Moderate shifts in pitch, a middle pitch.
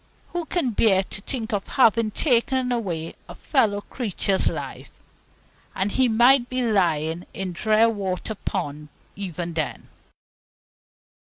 No: average, 4.7 semitones; high, 210 Hz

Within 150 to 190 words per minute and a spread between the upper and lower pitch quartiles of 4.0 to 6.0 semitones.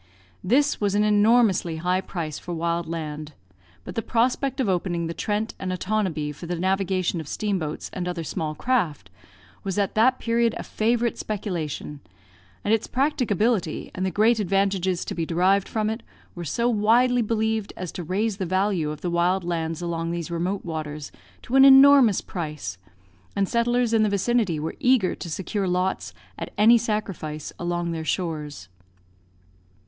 Yes: average, 165 wpm; average, 4.7 semitones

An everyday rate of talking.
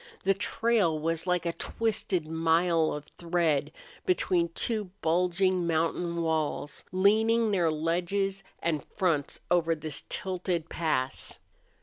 No: slow, 115 wpm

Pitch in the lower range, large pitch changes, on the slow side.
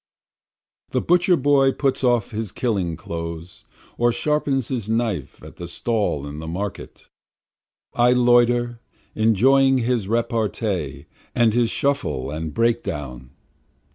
Yes: low, 115 Hz; wide, 6.2 semitones; slow, 130 wpm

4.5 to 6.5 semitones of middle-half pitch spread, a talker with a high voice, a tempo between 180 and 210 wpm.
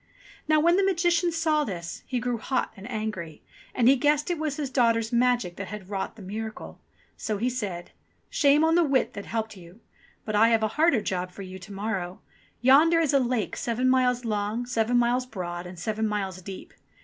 Yes: average, 4.9 semitones; high, 230 Hz; fast, 205 wpm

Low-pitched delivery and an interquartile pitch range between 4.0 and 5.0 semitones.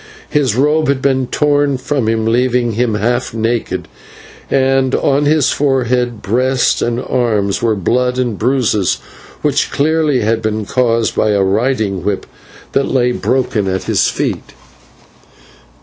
No: low, 125 Hz; average, 3.3 semitones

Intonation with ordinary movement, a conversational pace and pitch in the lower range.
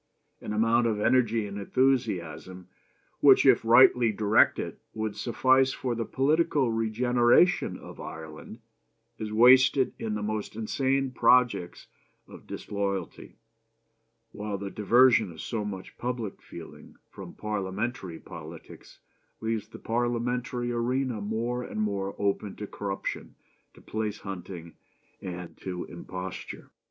No: average, 3.7 semitones; slow, 120 wpm; low, 110 Hz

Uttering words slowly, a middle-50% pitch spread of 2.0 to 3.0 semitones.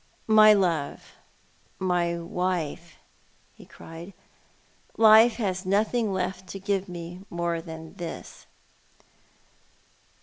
Yes: slow, 105 wpm; average, 2.7 semitones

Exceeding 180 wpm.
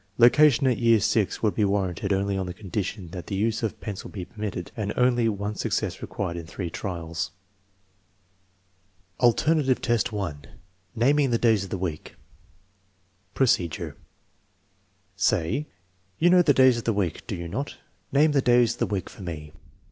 No: average, 170 wpm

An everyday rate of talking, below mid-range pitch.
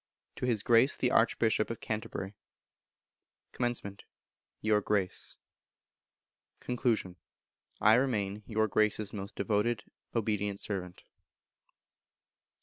No: slow, 90 wpm; low, 110 Hz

